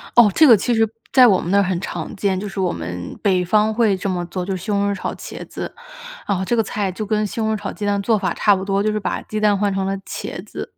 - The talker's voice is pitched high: Yes, high, 200 Hz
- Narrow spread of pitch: Yes, narrow, 2.0 semitones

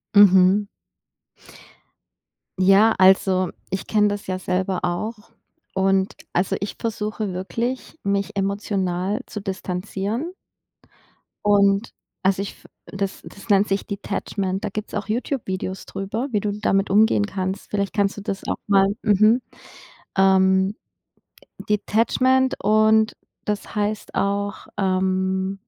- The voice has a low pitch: No, high, 200 Hz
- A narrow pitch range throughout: Yes, narrow, 1.8 semitones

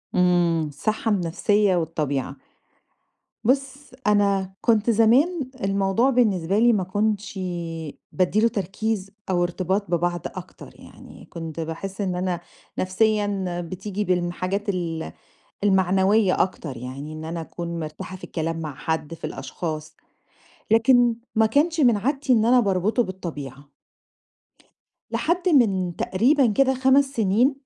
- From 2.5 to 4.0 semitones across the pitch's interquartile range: No, average, 4.6 semitones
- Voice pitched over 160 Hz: Yes, high, 190 Hz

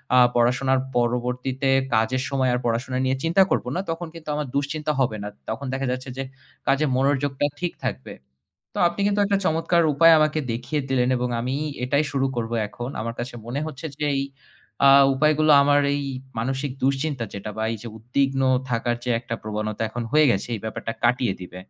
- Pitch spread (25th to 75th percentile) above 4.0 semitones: No, average, 3.4 semitones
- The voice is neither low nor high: No, low, 130 Hz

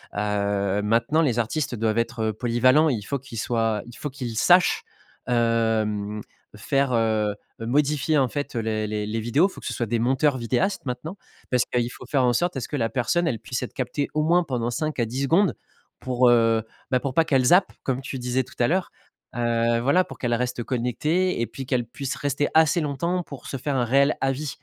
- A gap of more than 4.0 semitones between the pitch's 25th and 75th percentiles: No, average, 3.7 semitones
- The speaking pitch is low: Yes, low, 125 Hz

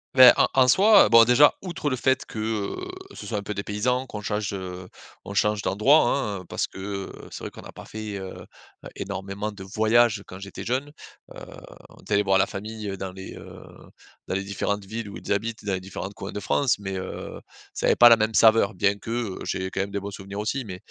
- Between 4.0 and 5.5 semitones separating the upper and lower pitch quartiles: No, average, 2.9 semitones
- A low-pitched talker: Yes, low, 105 Hz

